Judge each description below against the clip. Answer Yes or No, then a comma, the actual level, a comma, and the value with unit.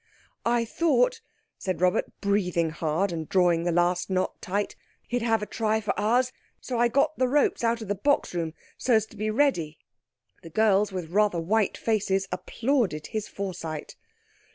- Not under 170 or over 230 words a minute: Yes, average, 175 wpm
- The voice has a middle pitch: No, high, 205 Hz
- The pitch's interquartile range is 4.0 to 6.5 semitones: Yes, average, 4.6 semitones